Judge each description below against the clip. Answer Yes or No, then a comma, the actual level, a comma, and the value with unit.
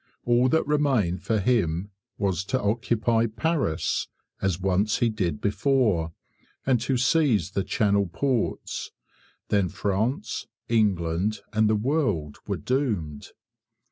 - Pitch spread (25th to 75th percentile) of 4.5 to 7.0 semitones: Yes, average, 4.8 semitones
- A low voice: Yes, low, 105 Hz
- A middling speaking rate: No, slow, 120 wpm